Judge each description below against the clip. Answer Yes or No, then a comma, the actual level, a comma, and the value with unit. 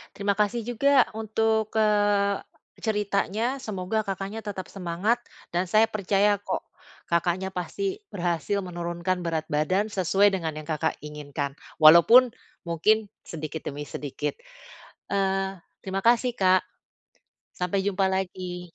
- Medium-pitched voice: No, high, 195 Hz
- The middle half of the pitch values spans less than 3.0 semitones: No, average, 3.6 semitones